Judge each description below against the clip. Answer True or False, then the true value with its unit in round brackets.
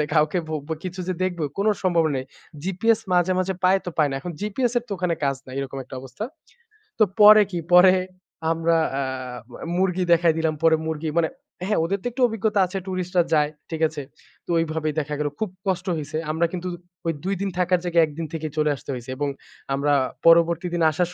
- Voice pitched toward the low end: False (170 Hz)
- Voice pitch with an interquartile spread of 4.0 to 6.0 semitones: False (3.2 semitones)